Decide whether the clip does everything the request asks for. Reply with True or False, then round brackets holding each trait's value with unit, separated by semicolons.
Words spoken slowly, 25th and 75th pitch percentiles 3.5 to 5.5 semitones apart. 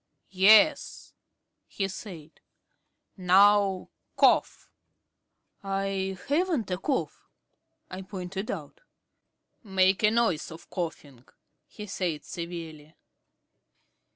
False (85 wpm; 2.8 semitones)